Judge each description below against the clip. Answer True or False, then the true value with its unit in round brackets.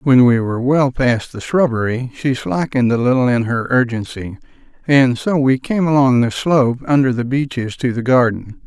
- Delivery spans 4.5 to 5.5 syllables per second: True (5.0 syllables/s)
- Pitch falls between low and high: False (125 Hz)